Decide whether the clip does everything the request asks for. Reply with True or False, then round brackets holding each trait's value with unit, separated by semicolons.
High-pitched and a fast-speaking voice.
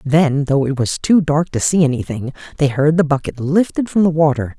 False (150 Hz; 220 wpm)